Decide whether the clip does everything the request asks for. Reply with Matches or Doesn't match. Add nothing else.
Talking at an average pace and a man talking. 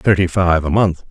Doesn't match